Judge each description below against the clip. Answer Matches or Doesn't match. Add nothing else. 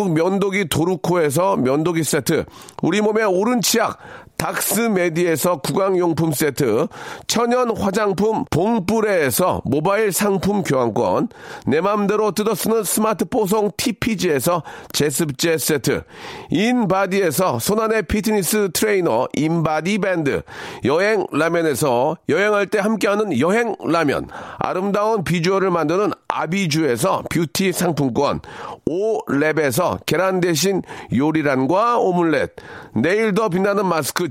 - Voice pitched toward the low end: Doesn't match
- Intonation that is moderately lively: Matches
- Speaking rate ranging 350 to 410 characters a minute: Doesn't match